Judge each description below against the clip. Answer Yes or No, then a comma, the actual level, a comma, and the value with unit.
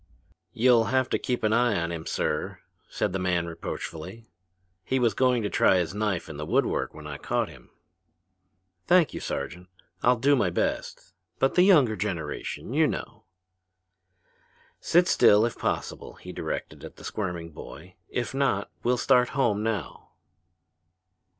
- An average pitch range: No, wide, 5.9 semitones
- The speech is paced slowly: No, average, 155 wpm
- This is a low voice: Yes, low, 110 Hz